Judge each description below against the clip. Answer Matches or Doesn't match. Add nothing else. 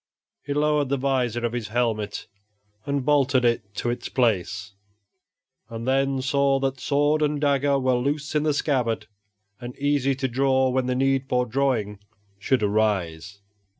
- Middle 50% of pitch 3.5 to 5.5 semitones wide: Doesn't match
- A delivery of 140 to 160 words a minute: Matches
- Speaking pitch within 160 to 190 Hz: Doesn't match